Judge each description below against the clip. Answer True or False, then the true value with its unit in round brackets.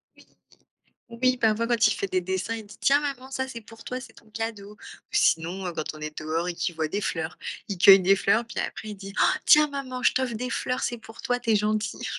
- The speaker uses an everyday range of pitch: True (4.6 semitones)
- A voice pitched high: True (215 Hz)